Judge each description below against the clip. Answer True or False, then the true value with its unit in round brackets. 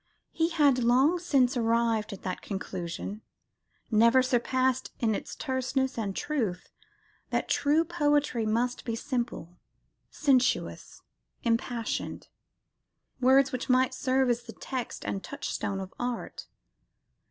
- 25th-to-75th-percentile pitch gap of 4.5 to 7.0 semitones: False (2.9 semitones)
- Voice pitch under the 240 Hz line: False (250 Hz)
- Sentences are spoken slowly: True (120 wpm)